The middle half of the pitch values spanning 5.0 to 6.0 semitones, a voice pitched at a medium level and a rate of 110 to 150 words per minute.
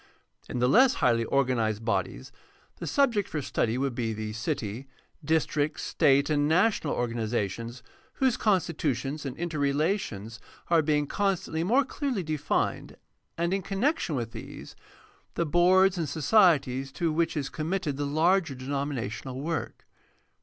Yes: wide, 5.6 semitones; medium, 150 Hz; slow, 135 wpm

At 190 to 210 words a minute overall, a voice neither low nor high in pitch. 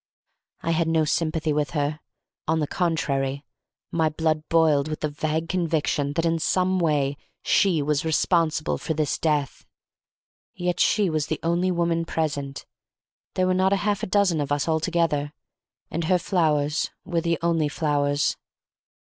No: average, 150 wpm; medium, 160 Hz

